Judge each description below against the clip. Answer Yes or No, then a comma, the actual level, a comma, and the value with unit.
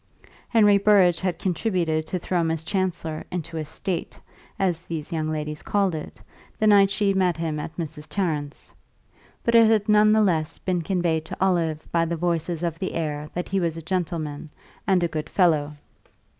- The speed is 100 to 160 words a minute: No, average, 185 wpm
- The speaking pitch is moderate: Yes, medium, 170 Hz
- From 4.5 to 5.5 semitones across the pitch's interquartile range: No, average, 3.3 semitones